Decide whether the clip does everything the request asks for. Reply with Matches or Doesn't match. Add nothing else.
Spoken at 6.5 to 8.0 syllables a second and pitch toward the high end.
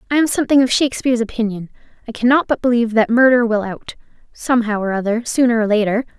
Matches